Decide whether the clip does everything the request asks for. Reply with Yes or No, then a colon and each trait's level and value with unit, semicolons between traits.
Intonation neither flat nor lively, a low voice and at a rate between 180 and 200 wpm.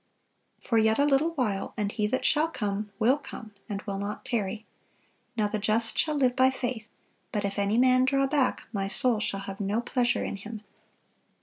No: average, 3.9 semitones; high, 220 Hz; average, 195 wpm